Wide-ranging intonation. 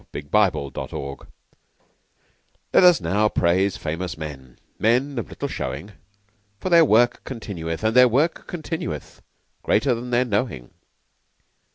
Yes: wide, 7.4 semitones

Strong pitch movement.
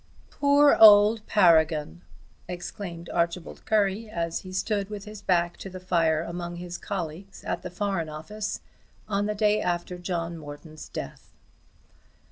No: average, 3.5 semitones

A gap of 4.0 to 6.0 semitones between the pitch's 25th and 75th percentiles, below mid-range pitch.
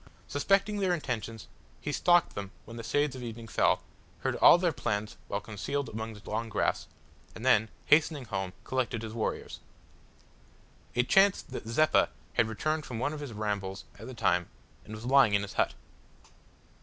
Yes: average, 5.2 semitones; low, 115 Hz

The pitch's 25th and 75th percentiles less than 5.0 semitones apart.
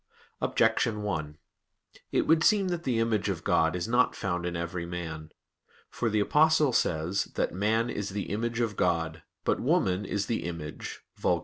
No: average, 5.3 semitones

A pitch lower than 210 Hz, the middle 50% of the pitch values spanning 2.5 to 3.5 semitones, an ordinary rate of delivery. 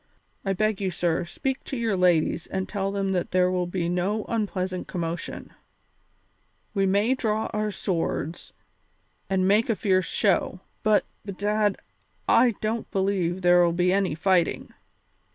Yes: high, 190 Hz; average, 2.8 semitones; average, 145 wpm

